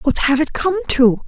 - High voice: Yes, very high, 275 Hz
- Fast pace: Yes, fast, 235 wpm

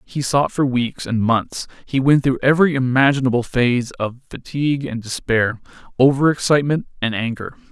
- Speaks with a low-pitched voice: Yes, low, 130 Hz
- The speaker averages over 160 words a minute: No, average, 155 wpm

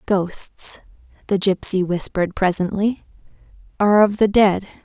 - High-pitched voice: Yes, high, 195 Hz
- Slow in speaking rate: Yes, slow, 110 wpm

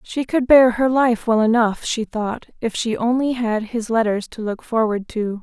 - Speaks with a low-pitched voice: No, high, 230 Hz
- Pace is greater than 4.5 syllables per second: No, 4.4 syllables/s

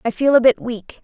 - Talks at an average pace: No, fast, 290 wpm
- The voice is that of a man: No, female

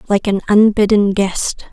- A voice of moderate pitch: No, high, 205 Hz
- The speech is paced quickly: No, average, 140 wpm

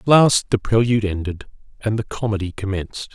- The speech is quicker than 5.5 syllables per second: Yes, 5.7 syllables/s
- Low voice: Yes, low, 105 Hz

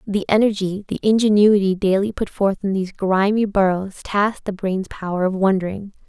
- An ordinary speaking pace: Yes, average, 170 wpm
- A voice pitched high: Yes, high, 195 Hz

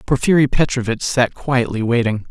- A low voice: Yes, low, 125 Hz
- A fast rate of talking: No, slow, 130 wpm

